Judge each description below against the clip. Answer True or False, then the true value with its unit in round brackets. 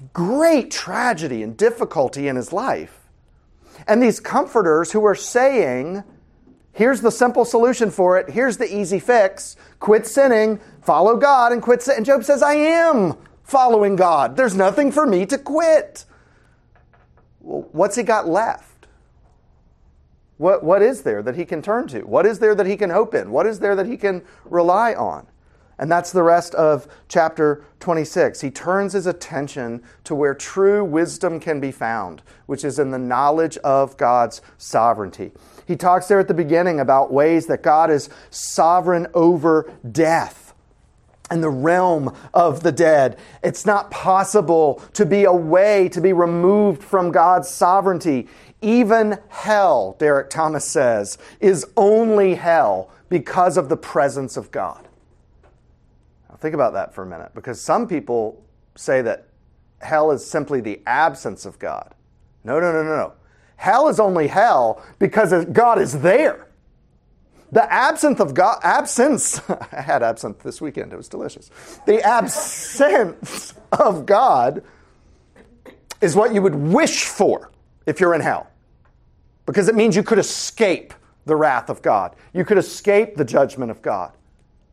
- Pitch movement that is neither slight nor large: False (6.2 semitones)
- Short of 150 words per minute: False (155 wpm)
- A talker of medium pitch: True (180 Hz)